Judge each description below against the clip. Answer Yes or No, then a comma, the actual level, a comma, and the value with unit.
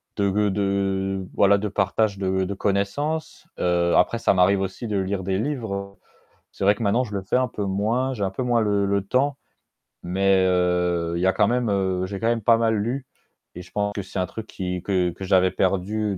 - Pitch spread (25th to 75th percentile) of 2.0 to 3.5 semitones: Yes, narrow, 2.5 semitones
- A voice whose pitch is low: Yes, low, 100 Hz